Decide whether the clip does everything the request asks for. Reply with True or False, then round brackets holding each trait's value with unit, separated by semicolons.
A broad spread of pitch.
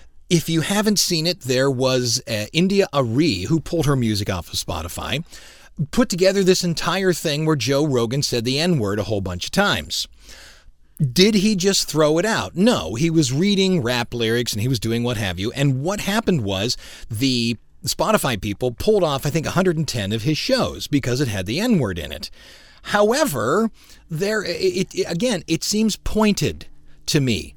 True (7.7 semitones)